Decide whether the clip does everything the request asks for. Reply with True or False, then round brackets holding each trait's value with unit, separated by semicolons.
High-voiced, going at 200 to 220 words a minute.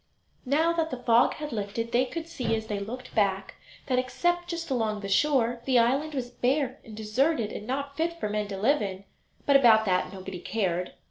True (240 Hz; 205 wpm)